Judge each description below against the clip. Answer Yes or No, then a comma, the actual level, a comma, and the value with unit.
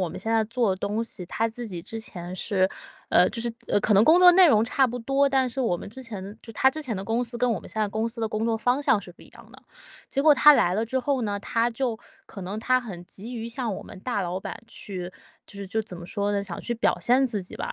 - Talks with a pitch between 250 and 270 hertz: No, high, 225 Hz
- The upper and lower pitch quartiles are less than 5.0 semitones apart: Yes, average, 3.7 semitones